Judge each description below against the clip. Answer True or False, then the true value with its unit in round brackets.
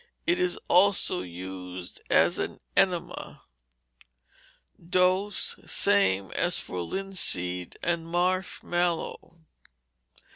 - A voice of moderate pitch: True (170 Hz)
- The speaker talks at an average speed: False (85 wpm)